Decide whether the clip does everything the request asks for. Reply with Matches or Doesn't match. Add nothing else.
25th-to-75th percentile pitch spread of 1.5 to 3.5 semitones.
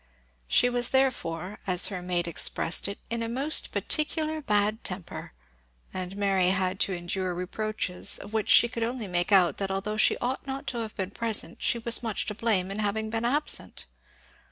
Doesn't match